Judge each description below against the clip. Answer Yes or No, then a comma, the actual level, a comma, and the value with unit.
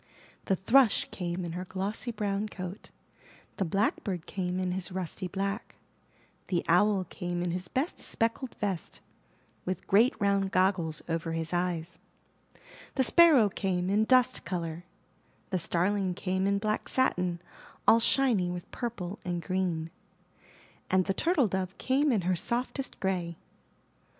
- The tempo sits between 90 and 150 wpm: Yes, average, 140 wpm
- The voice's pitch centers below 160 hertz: No, high, 190 Hz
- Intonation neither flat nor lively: Yes, average, 3.1 semitones